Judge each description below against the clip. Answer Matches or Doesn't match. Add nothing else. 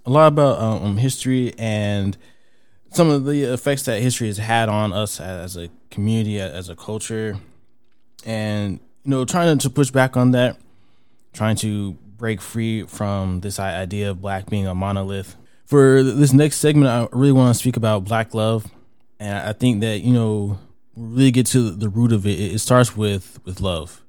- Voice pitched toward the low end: Matches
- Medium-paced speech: Matches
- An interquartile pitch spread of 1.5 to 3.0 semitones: Doesn't match